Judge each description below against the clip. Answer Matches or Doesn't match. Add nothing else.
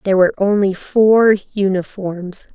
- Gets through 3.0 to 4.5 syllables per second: Matches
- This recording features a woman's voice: Matches